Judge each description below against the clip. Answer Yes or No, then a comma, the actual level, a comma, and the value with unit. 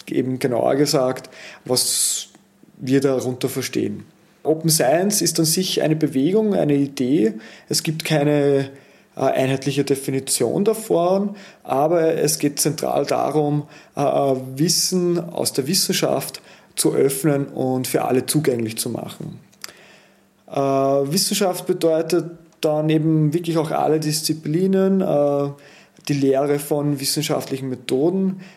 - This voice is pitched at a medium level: Yes, medium, 150 Hz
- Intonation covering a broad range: No, average, 3.5 semitones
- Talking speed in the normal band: No, slow, 120 wpm